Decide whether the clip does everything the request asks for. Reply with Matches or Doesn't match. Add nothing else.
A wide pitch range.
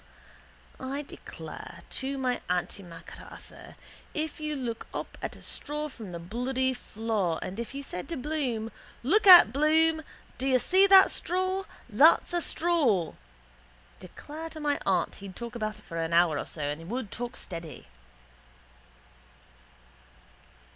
Matches